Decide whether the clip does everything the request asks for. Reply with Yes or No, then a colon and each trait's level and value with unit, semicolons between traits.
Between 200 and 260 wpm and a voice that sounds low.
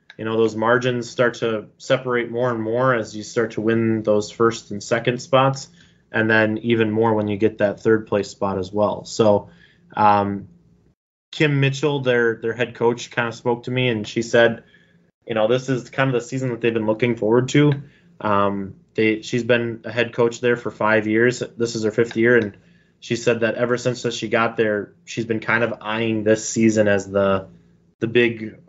Yes: fast, 205 wpm; low, 115 Hz